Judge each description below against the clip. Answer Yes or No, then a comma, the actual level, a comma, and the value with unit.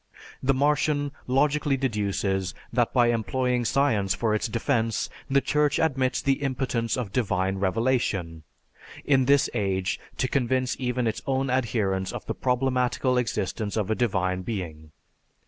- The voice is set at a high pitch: No, low, 120 Hz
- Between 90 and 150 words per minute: Yes, average, 140 wpm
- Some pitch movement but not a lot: Yes, average, 4.8 semitones